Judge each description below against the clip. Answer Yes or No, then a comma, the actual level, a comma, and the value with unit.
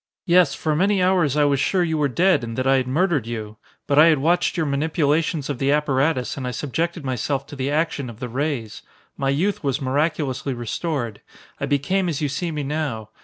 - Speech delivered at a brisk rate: Yes, fast, 215 wpm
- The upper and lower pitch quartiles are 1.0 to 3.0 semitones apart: No, average, 3.6 semitones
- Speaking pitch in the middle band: Yes, medium, 145 Hz